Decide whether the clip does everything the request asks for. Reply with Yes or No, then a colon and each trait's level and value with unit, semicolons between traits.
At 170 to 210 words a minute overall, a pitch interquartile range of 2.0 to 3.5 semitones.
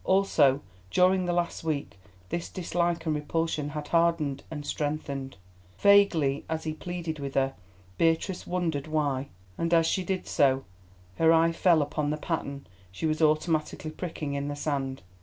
No: average, 160 wpm; average, 2.9 semitones